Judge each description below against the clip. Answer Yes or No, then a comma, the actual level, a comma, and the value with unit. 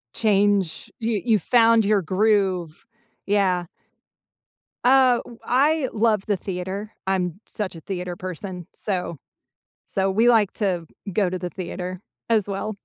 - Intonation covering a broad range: No, average, 3.2 semitones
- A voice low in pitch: No, high, 200 Hz